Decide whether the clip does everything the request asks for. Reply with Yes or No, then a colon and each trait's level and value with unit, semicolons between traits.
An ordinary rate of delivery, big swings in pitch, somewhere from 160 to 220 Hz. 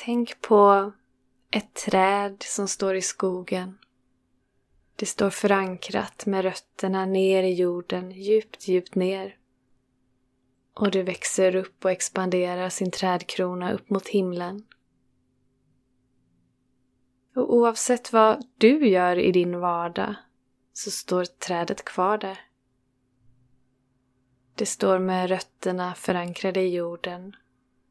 No: slow, 105 wpm; wide, 7.1 semitones; medium, 185 Hz